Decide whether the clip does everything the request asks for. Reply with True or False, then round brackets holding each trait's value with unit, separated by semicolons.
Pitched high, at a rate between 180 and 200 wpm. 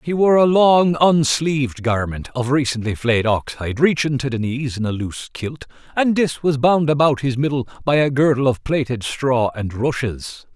False (135 Hz; 190 wpm)